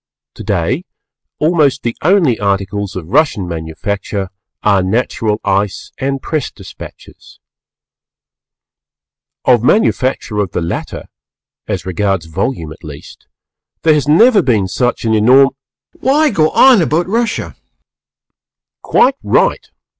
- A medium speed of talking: No, slow, 120 wpm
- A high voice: No, low, 120 Hz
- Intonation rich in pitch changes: Yes, wide, 8.1 semitones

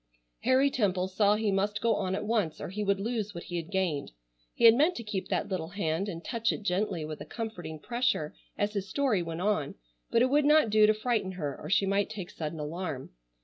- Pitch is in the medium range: No, high, 200 Hz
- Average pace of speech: No, fast, 230 wpm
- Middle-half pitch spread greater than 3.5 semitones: Yes, average, 4.2 semitones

